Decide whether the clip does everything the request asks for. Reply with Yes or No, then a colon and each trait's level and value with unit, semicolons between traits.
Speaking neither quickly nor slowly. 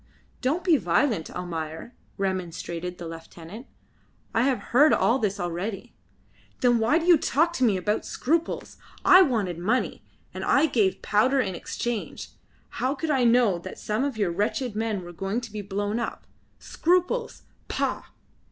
Yes: average, 160 wpm